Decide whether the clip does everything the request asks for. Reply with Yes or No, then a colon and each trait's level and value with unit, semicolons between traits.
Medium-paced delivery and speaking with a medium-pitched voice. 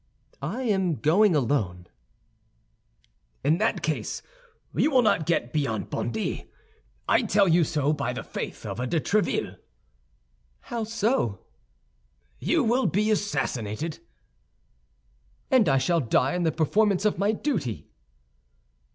No: slow, 125 wpm; medium, 170 Hz